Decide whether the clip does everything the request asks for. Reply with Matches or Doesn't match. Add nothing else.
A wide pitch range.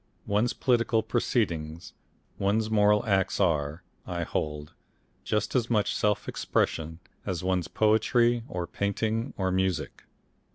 Doesn't match